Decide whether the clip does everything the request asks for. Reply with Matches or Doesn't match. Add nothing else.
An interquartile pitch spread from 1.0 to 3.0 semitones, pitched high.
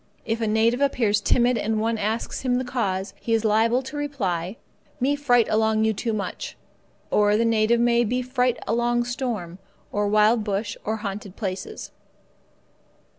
Matches